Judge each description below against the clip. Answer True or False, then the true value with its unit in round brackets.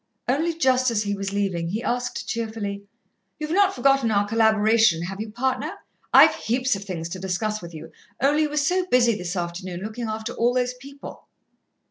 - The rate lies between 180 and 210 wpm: True (185 wpm)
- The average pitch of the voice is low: False (220 Hz)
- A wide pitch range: False (4.4 semitones)